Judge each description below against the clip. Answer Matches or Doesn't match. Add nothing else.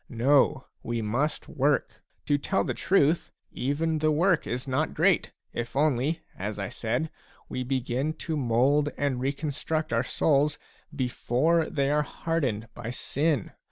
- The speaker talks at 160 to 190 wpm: Doesn't match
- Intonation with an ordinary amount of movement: Matches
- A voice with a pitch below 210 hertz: Matches